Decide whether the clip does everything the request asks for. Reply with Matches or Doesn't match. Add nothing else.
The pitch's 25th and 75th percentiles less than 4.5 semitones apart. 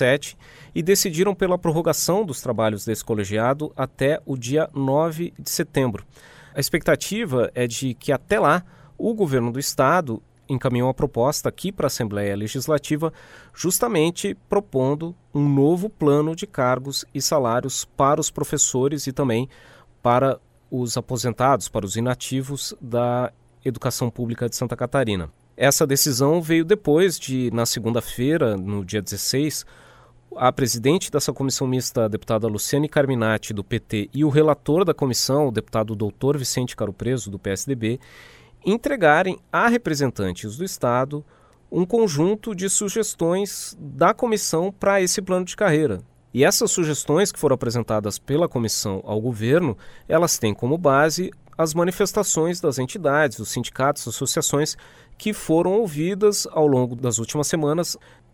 Doesn't match